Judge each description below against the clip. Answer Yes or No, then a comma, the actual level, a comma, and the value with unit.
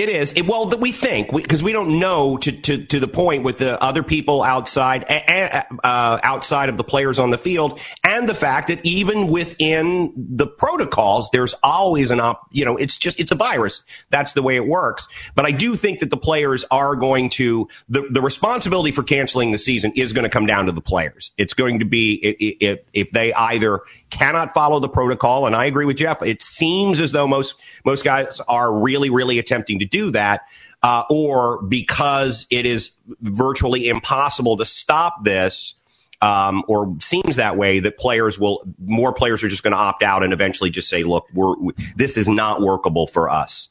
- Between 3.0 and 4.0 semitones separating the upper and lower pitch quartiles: No, average, 4.8 semitones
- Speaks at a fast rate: Yes, fast, 210 wpm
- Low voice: Yes, low, 130 Hz